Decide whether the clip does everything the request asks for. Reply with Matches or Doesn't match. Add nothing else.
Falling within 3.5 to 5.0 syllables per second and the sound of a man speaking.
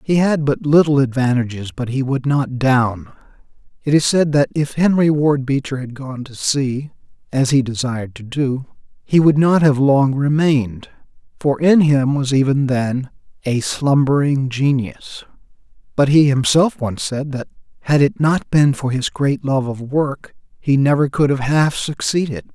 Matches